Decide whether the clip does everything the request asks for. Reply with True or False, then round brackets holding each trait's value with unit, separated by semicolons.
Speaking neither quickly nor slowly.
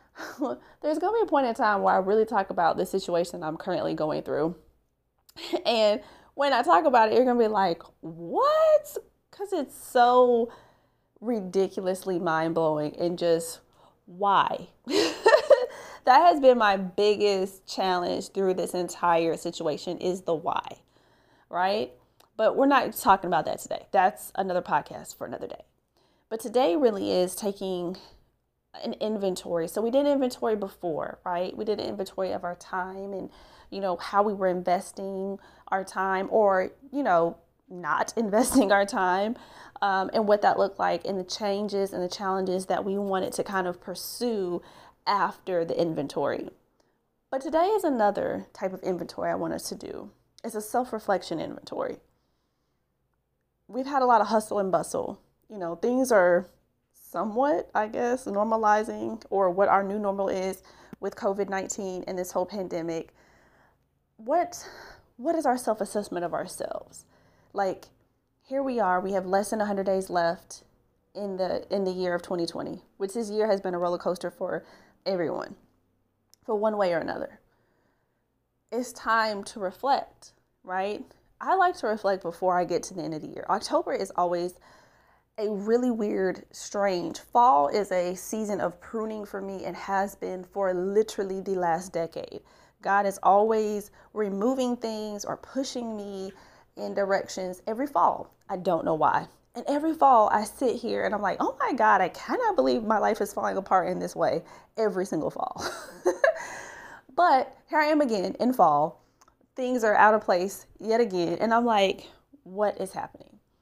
True (165 wpm)